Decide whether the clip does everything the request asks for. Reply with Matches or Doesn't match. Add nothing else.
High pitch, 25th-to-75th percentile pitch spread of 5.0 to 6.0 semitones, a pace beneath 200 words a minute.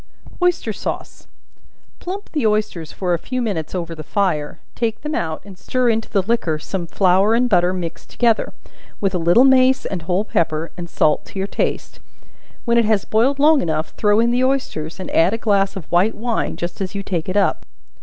Doesn't match